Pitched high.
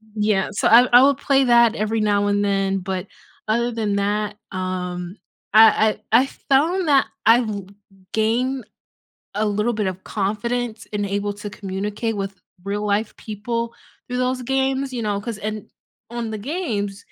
Yes: high, 215 Hz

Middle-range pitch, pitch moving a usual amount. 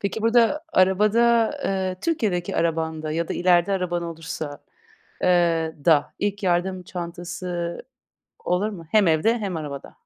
Yes: medium, 180 Hz; average, 3.3 semitones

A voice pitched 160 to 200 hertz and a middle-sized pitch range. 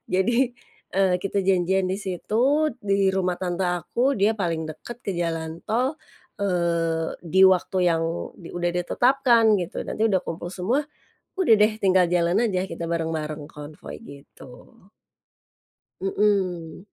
Yes: medium, 185 Hz; average, 3.0 semitones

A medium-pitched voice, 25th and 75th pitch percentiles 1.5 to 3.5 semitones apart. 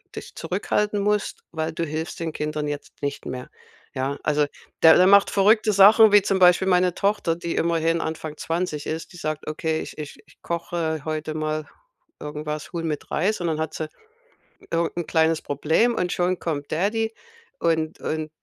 Yes: medium, 165 Hz; average, 2.9 semitones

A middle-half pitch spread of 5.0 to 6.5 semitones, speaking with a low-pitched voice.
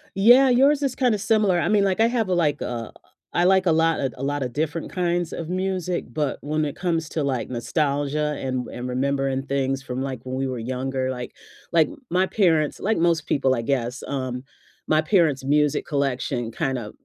No: average, 5.3 semitones; medium, 150 Hz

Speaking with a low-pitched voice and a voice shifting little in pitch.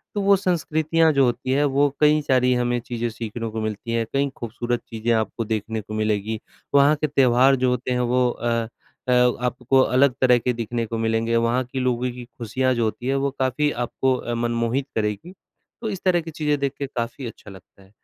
No: low, 125 Hz; average, 3.1 semitones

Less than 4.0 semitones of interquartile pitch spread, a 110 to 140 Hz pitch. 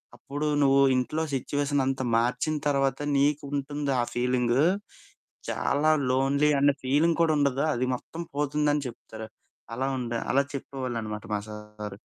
Yes: average, 2.8 semitones; low, 135 Hz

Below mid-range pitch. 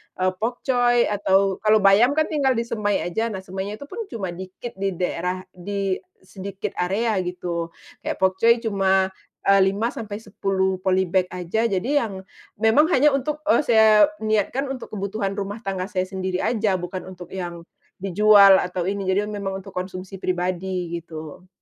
No: high, 195 Hz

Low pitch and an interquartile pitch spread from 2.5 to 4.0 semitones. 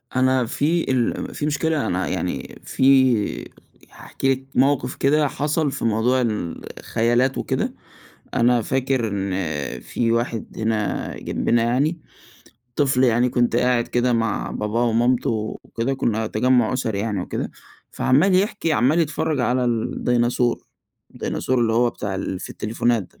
Yes: low, 120 Hz; average, 2.9 semitones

